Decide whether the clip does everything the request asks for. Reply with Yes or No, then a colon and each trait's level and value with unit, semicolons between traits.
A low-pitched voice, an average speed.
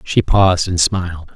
Yes: very low, 85 Hz; average, 175 wpm